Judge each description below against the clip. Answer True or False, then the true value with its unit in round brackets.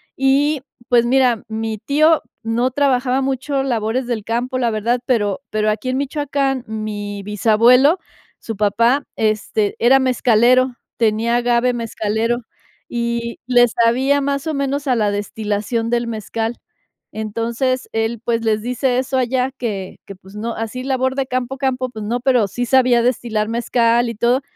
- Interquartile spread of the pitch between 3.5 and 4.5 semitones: False (2.8 semitones)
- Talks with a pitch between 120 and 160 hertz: False (240 Hz)